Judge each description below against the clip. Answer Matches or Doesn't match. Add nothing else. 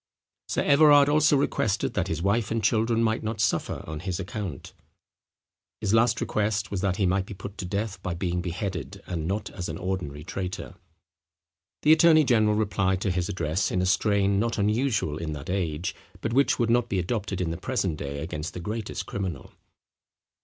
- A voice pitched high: Doesn't match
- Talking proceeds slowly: Doesn't match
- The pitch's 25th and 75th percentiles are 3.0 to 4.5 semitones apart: Matches